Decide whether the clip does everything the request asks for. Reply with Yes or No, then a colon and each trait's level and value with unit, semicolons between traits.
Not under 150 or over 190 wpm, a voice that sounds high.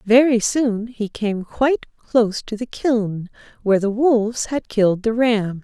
Yes: average, 170 wpm; high, 225 Hz